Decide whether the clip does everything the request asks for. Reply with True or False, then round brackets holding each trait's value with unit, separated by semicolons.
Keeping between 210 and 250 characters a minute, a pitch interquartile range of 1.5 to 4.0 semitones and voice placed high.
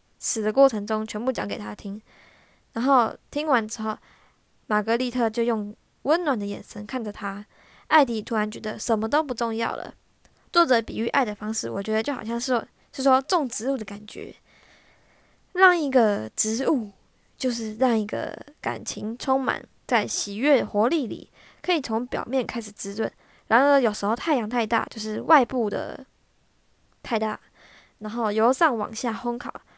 True (240 characters per minute; 3.4 semitones; 230 Hz)